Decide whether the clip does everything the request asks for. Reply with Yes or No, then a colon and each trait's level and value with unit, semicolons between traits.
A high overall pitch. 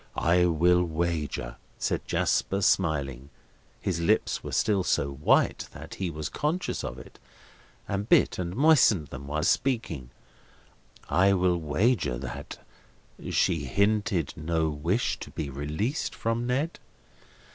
No: very low, 85 Hz